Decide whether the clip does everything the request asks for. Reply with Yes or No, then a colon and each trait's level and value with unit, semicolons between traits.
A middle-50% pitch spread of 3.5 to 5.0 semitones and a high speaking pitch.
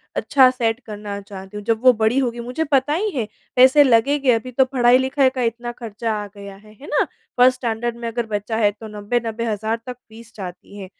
No: average, 3.0 semitones; high, 230 Hz